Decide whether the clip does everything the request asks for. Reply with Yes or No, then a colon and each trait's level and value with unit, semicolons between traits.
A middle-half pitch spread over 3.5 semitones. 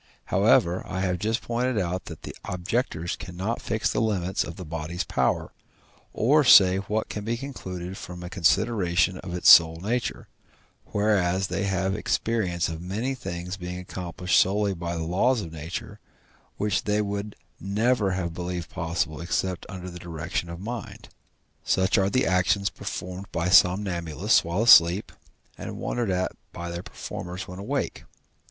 No: average, 3.0 semitones